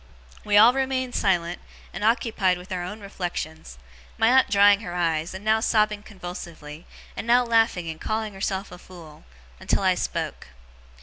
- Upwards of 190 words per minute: No, average, 165 wpm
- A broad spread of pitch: No, average, 3.9 semitones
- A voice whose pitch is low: No, high, 200 Hz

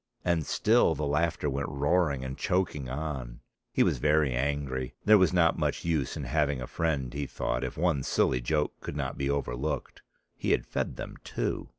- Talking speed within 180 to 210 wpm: Yes, average, 190 wpm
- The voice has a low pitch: Yes, very low, 70 Hz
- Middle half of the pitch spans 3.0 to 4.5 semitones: Yes, average, 3.3 semitones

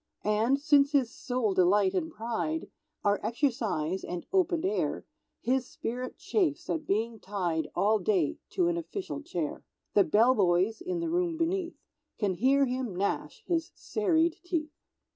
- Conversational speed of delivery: Yes, average, 150 wpm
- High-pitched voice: Yes, very high, 255 Hz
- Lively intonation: Yes, wide, 8.2 semitones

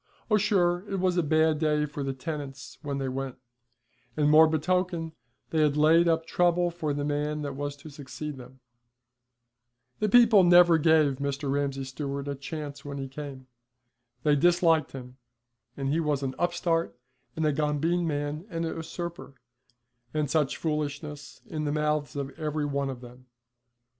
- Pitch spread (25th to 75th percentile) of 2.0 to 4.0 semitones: Yes, average, 2.8 semitones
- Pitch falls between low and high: Yes, medium, 150 Hz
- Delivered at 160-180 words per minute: Yes, average, 170 wpm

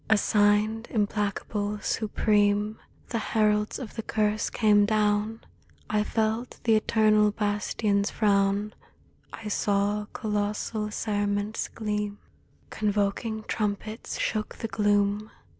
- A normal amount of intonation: No, narrow, 1.0 semitones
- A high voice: Yes, high, 210 Hz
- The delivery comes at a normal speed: No, slow, 100 wpm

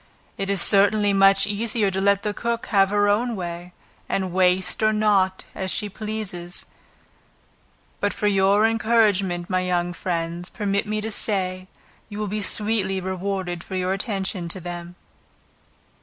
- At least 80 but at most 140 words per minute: No, average, 155 wpm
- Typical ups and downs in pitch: No, narrow, 2.2 semitones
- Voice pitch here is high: Yes, high, 195 Hz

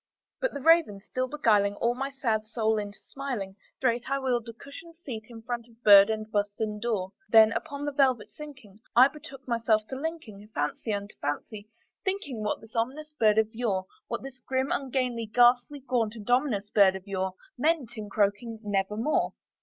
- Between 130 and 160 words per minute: No, average, 185 wpm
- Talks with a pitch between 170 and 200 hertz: No, high, 230 Hz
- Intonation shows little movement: No, average, 4.0 semitones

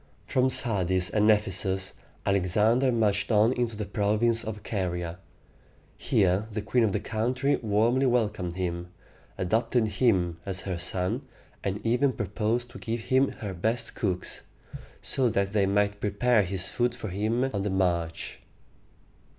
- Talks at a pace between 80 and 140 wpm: No, average, 150 wpm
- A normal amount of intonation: Yes, average, 3.6 semitones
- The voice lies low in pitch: Yes, low, 105 Hz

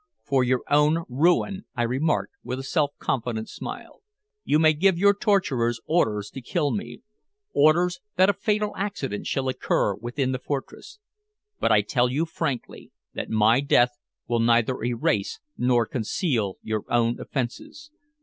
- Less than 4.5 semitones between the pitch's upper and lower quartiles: No, wide, 5.6 semitones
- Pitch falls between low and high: No, low, 130 Hz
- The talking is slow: No, average, 150 wpm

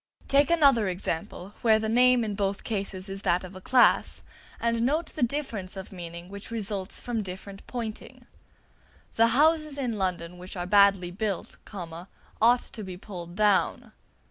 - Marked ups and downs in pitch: No, average, 4.2 semitones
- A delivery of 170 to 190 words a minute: No, average, 160 wpm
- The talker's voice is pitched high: Yes, high, 205 Hz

